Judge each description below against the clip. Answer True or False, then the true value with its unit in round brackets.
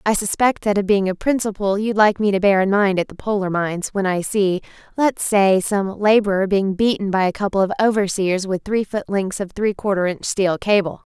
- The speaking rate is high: True (225 wpm)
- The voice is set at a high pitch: True (200 Hz)